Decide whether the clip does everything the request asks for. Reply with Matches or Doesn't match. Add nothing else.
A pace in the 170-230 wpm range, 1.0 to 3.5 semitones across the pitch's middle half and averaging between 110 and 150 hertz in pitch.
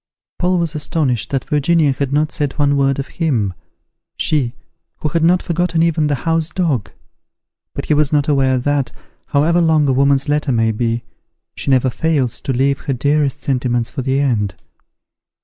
Matches